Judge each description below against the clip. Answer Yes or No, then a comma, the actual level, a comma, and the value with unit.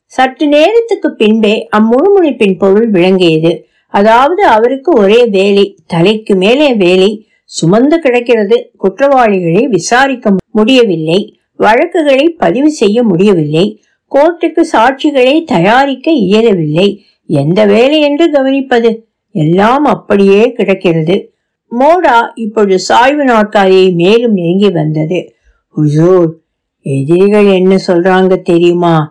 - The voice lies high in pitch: Yes, high, 210 Hz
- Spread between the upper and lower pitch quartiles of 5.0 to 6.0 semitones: Yes, wide, 5.6 semitones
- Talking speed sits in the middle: Yes, average, 90 wpm